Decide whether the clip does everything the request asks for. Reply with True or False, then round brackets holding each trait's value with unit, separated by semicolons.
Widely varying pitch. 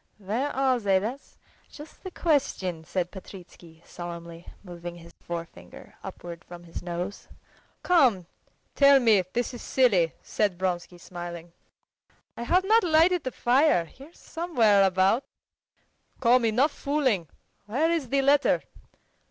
True (8.0 semitones)